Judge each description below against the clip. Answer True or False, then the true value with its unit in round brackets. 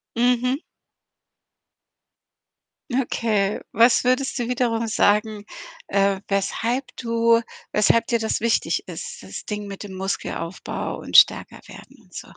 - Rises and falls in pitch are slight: False (3.2 semitones)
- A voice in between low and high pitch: False (230 Hz)